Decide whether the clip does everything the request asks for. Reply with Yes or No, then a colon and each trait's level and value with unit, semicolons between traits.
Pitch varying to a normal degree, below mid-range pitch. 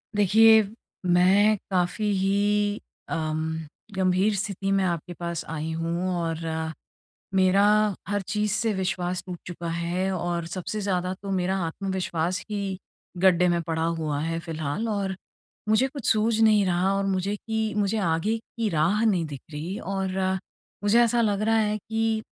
No: average, 3.3 semitones; high, 190 Hz